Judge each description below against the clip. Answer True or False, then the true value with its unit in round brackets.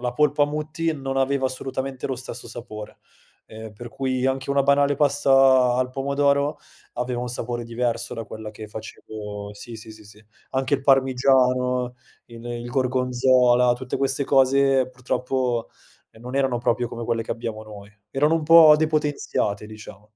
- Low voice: True (125 Hz)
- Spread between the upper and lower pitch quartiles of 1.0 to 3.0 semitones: True (2.6 semitones)